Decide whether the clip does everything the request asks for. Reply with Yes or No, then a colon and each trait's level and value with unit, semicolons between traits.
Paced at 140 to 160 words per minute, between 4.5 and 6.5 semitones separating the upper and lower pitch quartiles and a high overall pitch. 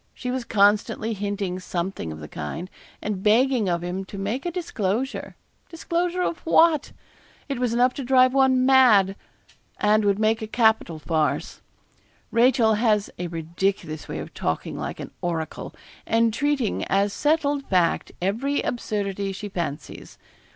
Yes: average, 150 wpm; average, 5.3 semitones; high, 215 Hz